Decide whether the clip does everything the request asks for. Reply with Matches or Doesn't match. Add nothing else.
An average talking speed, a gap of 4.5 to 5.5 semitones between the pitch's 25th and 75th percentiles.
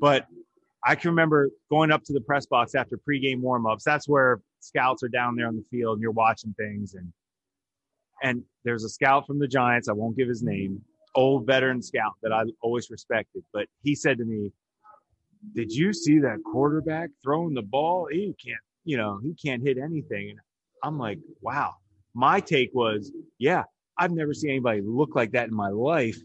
Matches